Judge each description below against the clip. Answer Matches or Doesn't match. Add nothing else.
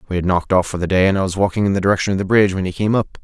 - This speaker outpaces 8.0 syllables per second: Matches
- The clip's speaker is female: Doesn't match